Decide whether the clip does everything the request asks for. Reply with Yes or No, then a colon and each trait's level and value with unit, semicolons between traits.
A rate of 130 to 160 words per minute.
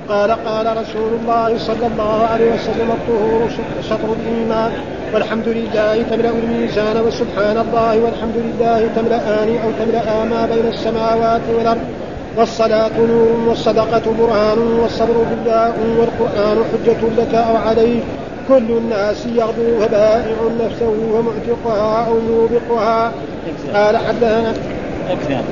No: average, 115 wpm